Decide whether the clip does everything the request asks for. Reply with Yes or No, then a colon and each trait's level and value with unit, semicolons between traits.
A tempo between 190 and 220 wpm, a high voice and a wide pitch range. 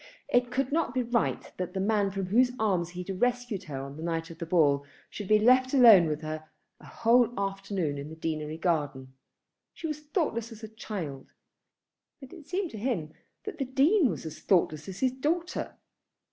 Yes: average, 200 wpm; high, 205 Hz; wide, 7.5 semitones